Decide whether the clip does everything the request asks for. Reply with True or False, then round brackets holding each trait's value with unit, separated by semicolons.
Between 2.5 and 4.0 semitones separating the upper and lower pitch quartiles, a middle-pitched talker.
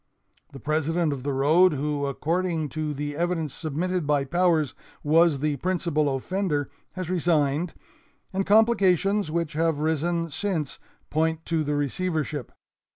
True (3.2 semitones; 160 Hz)